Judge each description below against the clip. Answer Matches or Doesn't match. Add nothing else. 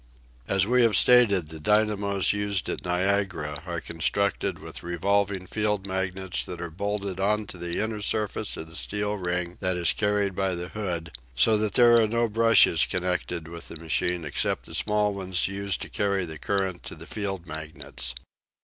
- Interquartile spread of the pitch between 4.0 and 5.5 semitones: Doesn't match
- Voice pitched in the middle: Doesn't match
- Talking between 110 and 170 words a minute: Doesn't match